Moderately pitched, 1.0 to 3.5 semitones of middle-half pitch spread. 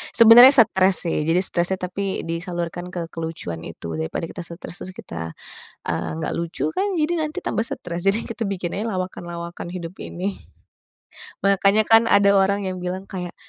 Yes: medium, 180 Hz; average, 2.9 semitones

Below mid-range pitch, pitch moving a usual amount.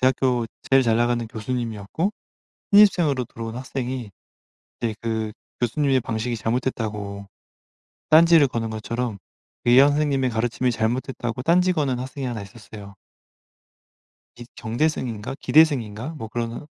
Yes: low, 120 Hz; average, 3.2 semitones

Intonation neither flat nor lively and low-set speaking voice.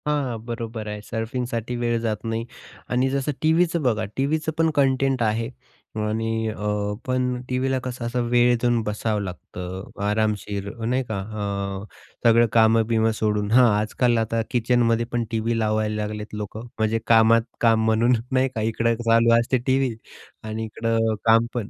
No: narrow, 2.3 semitones; low, 115 Hz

